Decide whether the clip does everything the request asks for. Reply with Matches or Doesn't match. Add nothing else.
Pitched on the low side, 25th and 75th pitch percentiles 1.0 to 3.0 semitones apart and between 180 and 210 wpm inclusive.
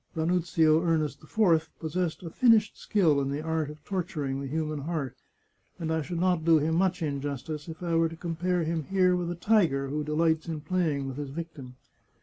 Doesn't match